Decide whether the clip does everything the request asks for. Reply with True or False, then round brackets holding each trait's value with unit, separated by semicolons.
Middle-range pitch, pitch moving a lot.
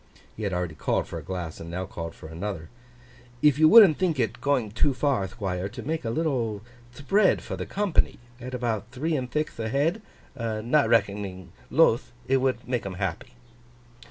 False (120 Hz; 6.4 semitones)